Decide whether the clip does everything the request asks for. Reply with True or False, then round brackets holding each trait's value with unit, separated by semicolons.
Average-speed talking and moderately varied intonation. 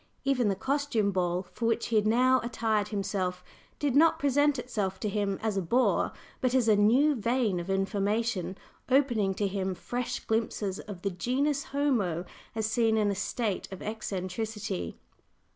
True (165 wpm; 4.3 semitones)